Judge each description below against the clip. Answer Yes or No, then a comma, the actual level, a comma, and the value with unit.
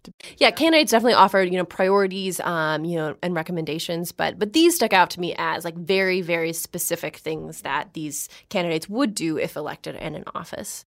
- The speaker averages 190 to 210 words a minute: Yes, average, 200 wpm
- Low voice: No, medium, 180 Hz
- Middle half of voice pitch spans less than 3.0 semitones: No, average, 3.3 semitones